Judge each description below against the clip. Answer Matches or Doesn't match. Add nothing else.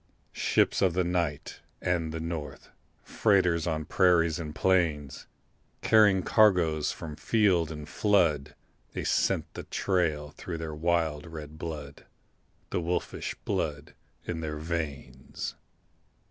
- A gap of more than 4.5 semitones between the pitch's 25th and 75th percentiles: Doesn't match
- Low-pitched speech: Matches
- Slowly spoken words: Matches